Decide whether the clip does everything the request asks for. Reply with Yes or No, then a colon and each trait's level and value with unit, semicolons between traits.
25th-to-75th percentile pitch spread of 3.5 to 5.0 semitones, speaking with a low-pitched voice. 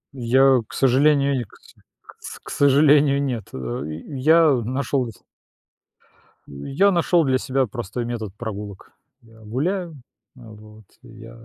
Yes: average, 4.0 semitones; low, 130 Hz